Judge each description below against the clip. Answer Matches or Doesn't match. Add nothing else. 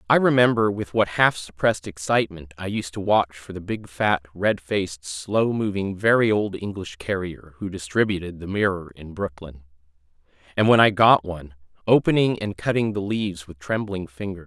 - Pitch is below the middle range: Matches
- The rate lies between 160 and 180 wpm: Matches